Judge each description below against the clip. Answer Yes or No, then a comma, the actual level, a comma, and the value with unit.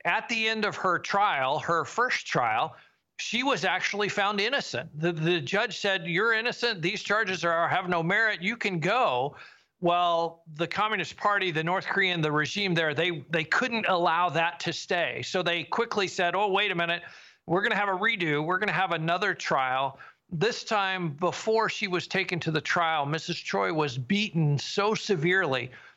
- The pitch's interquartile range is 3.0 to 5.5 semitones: Yes, average, 3.5 semitones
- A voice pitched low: No, medium, 180 Hz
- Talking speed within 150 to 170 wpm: No, average, 185 wpm